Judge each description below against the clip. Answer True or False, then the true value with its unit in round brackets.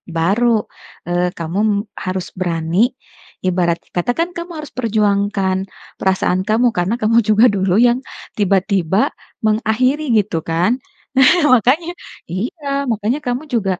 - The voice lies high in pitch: True (205 Hz)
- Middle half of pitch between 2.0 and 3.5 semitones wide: False (4.8 semitones)